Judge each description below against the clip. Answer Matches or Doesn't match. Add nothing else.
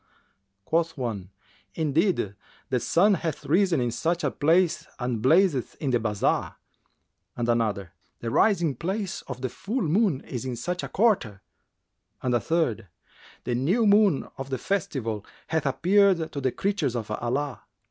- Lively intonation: Matches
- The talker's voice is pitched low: Doesn't match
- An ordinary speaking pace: Matches